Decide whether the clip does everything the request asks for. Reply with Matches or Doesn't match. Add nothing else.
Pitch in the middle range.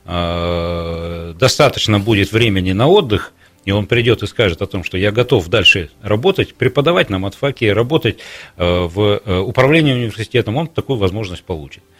Doesn't match